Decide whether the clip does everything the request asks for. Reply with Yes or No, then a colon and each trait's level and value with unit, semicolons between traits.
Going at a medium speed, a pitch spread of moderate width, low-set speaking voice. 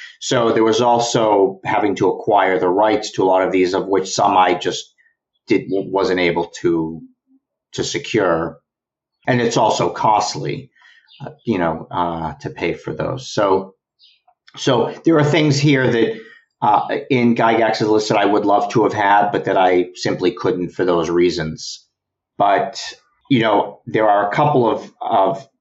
No: average, 170 wpm; wide, 7.7 semitones; low, 115 Hz